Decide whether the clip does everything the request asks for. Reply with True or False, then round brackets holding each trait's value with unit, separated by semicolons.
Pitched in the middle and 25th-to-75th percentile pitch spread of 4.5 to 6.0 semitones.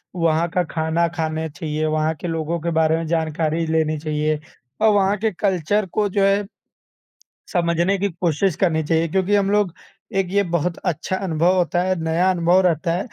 False (170 Hz; 2.9 semitones)